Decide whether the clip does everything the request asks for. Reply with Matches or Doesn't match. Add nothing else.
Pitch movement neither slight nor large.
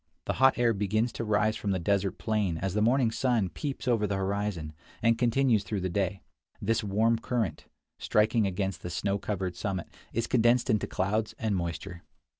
Matches